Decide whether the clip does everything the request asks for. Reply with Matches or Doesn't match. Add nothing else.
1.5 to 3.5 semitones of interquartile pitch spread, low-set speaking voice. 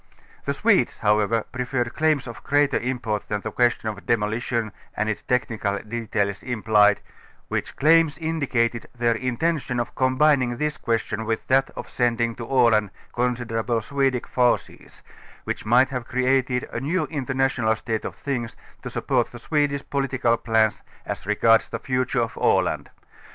Matches